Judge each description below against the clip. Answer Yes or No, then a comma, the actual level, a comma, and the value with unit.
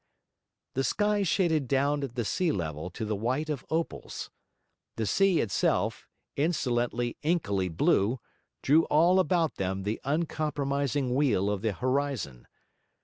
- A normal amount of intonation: No, wide, 6.3 semitones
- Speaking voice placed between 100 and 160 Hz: Yes, low, 135 Hz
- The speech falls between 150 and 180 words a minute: No, slow, 135 wpm